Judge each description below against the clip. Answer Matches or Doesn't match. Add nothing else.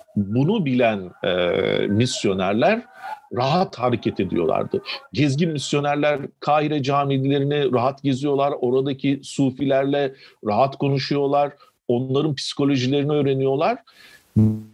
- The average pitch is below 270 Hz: Matches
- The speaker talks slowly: Matches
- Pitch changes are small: Matches